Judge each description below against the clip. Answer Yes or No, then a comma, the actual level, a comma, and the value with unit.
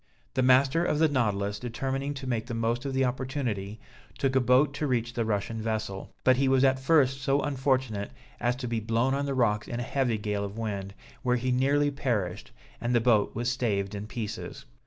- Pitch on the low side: Yes, low, 125 Hz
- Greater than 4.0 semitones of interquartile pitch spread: No, average, 3.5 semitones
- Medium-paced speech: No, fast, 210 wpm